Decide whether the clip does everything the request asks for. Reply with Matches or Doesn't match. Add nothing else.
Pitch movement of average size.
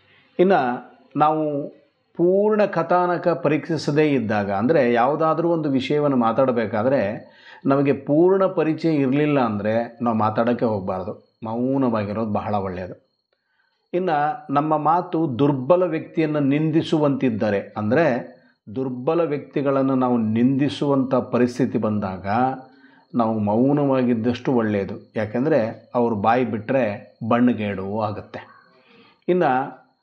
Matches